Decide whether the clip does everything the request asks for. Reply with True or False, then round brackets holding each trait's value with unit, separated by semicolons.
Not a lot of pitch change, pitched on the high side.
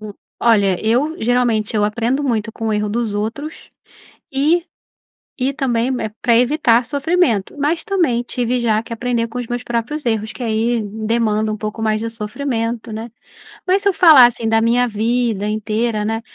True (2.3 semitones; 230 Hz)